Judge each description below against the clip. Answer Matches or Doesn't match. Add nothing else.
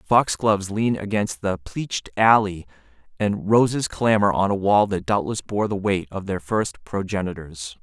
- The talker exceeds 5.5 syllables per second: Doesn't match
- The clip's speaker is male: Matches